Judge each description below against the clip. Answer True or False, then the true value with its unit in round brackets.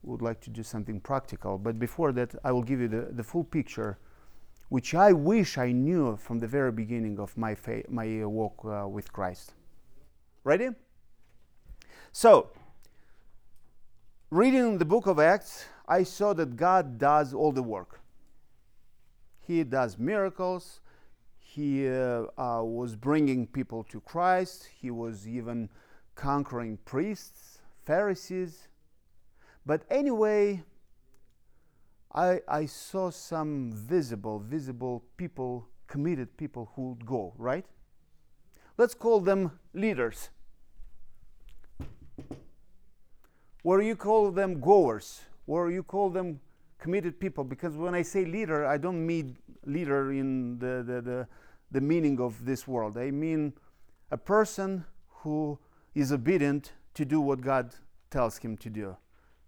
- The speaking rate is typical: False (130 wpm)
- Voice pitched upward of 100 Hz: True (140 Hz)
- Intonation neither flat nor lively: False (6.9 semitones)